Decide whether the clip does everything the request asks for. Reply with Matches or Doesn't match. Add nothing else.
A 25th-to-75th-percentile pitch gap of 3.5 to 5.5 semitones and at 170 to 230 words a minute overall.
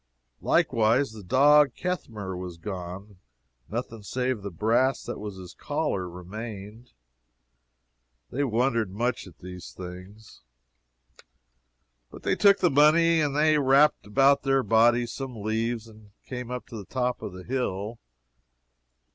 Doesn't match